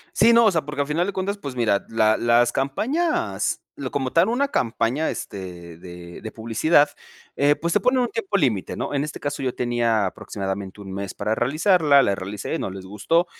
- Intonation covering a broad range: Yes, wide, 8.5 semitones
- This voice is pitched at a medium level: No, low, 125 Hz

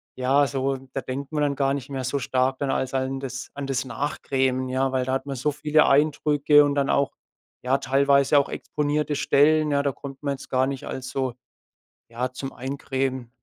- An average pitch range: No, narrow, 1.4 semitones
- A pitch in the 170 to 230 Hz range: No, low, 135 Hz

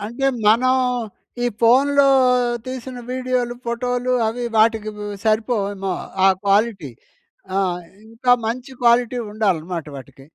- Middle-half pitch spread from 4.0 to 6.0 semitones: No, average, 3.1 semitones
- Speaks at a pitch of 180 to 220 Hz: No, high, 235 Hz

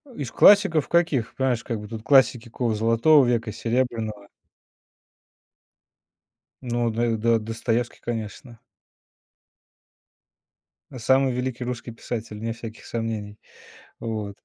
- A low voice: Yes, low, 115 Hz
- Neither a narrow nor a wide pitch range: No, narrow, 2.0 semitones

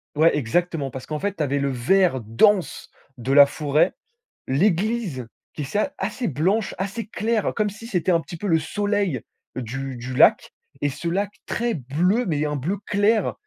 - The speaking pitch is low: No, medium, 170 Hz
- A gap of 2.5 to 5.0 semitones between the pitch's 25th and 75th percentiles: No, wide, 6.6 semitones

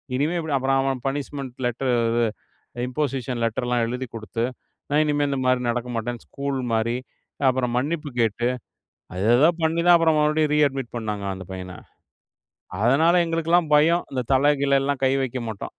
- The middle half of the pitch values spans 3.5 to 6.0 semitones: Yes, average, 3.8 semitones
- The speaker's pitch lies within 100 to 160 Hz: Yes, low, 135 Hz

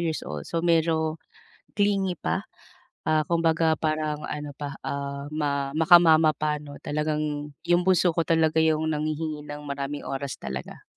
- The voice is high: No, medium, 155 Hz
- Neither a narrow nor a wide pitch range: No, narrow, 1.8 semitones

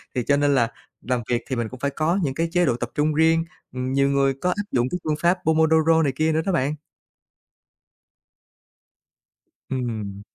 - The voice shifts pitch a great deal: No, average, 4.1 semitones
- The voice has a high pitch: No, medium, 140 Hz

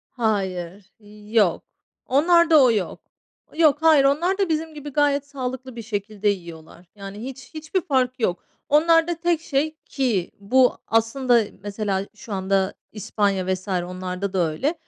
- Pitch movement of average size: No, wide, 6.9 semitones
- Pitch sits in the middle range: No, high, 235 Hz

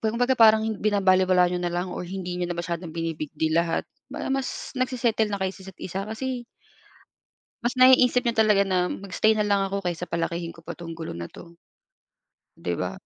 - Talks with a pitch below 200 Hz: Yes, high, 190 Hz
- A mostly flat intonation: No, average, 4.1 semitones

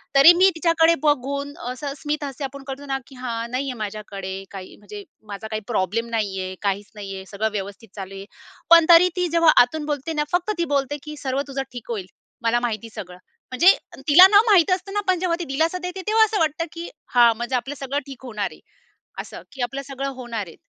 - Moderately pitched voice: No, very high, 270 Hz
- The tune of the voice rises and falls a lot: Yes, wide, 6.9 semitones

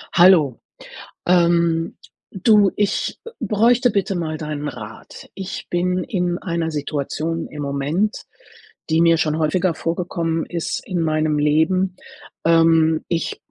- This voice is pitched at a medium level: Yes, medium, 165 Hz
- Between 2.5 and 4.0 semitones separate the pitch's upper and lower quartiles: Yes, average, 2.8 semitones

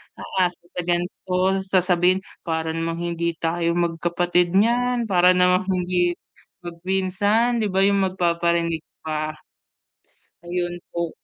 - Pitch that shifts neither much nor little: No, narrow, 1.8 semitones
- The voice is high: No, medium, 175 Hz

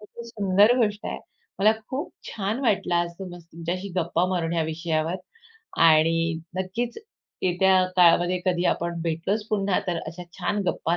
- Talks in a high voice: No, medium, 180 Hz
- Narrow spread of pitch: No, average, 3.1 semitones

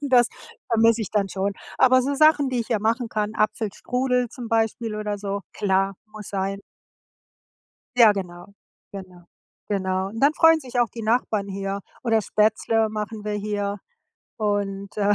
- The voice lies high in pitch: Yes, high, 215 Hz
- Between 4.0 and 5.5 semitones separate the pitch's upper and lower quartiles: No, average, 2.7 semitones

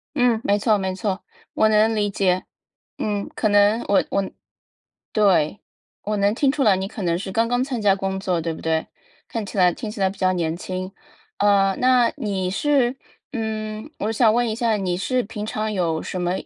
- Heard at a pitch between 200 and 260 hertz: Yes, high, 205 Hz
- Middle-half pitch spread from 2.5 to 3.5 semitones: Yes, average, 2.9 semitones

